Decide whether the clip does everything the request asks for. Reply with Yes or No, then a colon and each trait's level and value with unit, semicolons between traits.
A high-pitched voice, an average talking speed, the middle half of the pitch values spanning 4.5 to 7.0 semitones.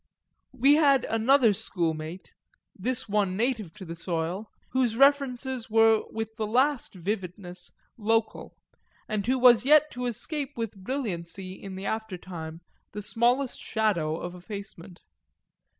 No: high, 220 Hz; slow, 130 wpm; average, 5.2 semitones